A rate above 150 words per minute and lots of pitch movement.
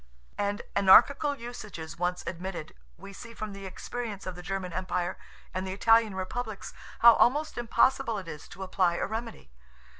No: average, 160 wpm; average, 3.8 semitones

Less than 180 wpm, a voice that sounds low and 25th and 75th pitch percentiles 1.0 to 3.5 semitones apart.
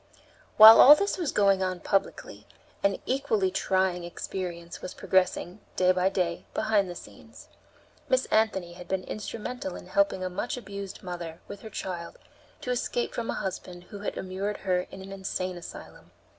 No: average, 170 wpm; high, 190 Hz; narrow, 2.6 semitones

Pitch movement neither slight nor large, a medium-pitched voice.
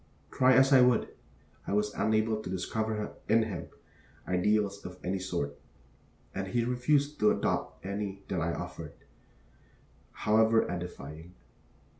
No: average, 3.5 semitones; low, 105 Hz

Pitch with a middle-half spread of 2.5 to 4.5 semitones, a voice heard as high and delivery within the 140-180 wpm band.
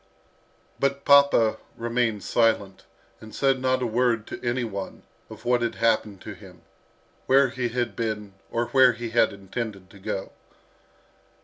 No: average, 2.8 semitones; low, 115 Hz; average, 150 wpm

